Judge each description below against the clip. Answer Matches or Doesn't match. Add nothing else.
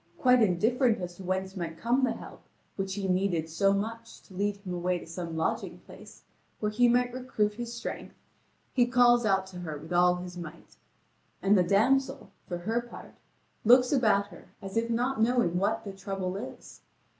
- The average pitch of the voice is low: Doesn't match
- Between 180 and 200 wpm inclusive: Matches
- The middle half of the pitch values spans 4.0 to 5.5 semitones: Matches